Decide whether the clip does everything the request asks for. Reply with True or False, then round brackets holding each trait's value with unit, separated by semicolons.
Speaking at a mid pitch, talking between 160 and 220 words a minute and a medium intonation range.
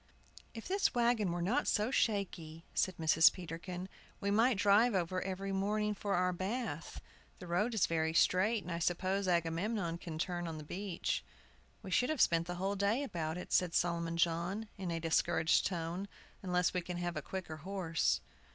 True (180 Hz; 185 wpm; 3.1 semitones)